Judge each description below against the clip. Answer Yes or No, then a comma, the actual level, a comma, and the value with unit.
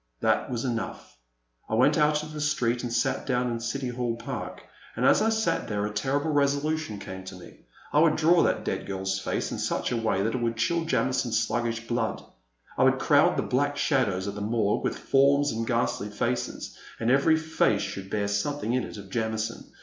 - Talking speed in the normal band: No, fast, 210 wpm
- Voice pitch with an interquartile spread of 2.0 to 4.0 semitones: No, average, 4.7 semitones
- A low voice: Yes, low, 120 Hz